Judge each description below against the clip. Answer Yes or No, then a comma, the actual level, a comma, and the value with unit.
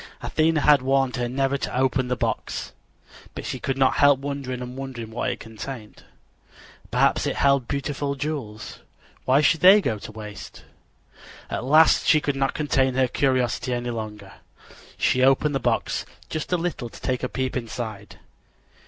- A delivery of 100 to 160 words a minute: No, average, 170 wpm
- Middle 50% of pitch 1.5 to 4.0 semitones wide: Yes, narrow, 2.5 semitones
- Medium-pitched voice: No, low, 130 Hz